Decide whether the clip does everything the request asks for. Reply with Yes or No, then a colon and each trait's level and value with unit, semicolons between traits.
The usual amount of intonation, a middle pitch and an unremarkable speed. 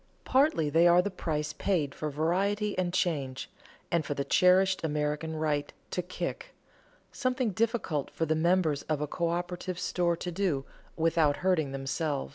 Yes: average, 3.5 semitones; medium, 165 Hz; average, 155 wpm